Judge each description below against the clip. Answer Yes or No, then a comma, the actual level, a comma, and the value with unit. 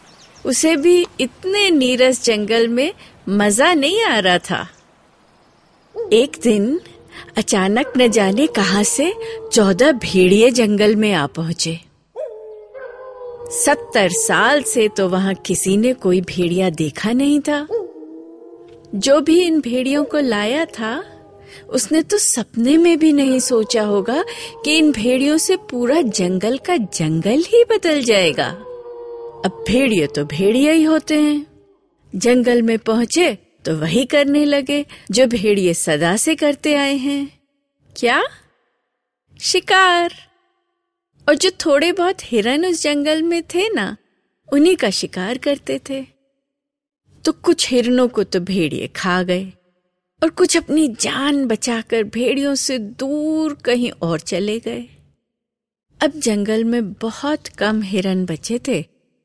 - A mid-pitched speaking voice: No, very high, 260 Hz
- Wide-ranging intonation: Yes, wide, 7.1 semitones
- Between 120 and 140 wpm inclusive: Yes, average, 130 wpm